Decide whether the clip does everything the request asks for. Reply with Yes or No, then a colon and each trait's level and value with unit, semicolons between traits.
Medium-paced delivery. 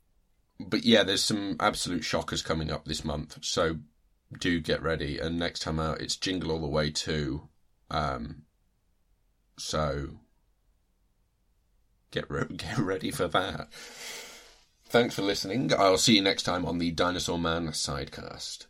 Yes: average, 145 wpm